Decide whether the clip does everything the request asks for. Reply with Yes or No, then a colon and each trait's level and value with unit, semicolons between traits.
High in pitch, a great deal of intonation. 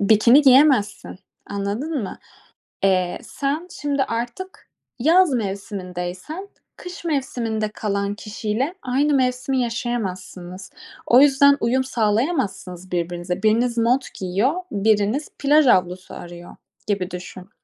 Yes: high, 225 Hz; wide, 6.0 semitones